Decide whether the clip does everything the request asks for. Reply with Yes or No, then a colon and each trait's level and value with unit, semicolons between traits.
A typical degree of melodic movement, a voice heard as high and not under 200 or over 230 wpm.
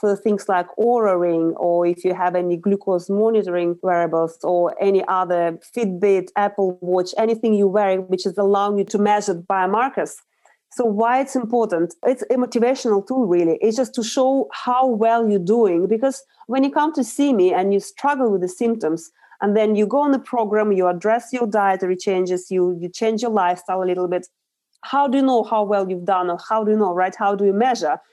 Yes: average, 4.2 semitones; high, 200 Hz; fast, 205 wpm